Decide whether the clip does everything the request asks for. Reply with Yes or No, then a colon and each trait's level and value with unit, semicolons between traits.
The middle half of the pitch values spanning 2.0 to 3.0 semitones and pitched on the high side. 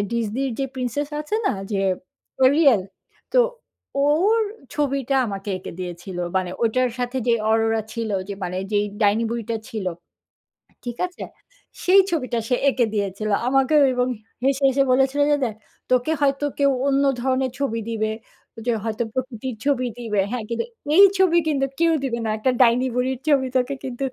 No: average, 3.7 semitones; very high, 250 Hz